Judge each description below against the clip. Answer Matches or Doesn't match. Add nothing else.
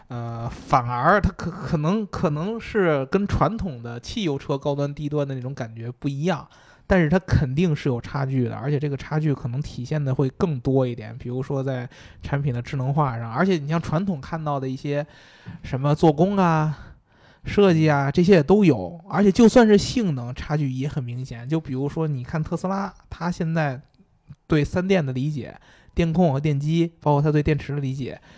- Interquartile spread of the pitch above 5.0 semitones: Doesn't match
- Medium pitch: Matches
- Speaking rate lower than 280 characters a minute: Doesn't match